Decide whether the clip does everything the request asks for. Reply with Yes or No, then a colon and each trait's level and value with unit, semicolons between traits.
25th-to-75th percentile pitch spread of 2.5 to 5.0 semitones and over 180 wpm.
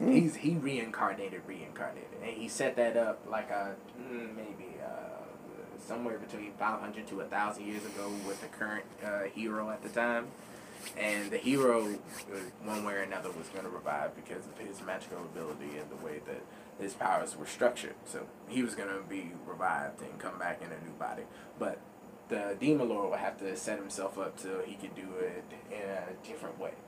Yes: average, 3.6 semitones; average, 190 wpm